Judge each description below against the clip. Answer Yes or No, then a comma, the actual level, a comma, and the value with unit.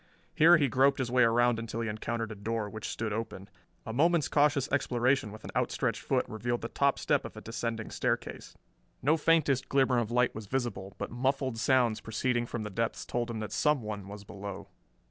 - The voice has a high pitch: No, low, 120 Hz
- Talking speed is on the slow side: No, average, 200 wpm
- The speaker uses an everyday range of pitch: Yes, average, 3.4 semitones